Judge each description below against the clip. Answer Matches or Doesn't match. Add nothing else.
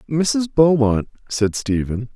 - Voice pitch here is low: Matches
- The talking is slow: Matches